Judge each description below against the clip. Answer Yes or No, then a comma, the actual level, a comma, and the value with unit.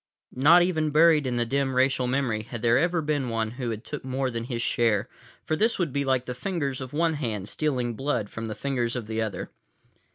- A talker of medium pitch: No, low, 130 Hz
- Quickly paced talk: Yes, fast, 220 wpm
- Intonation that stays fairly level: No, average, 4.1 semitones